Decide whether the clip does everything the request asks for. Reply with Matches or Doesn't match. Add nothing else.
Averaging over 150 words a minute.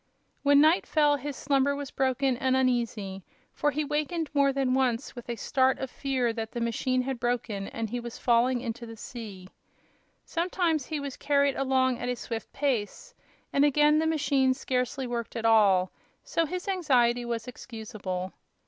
Matches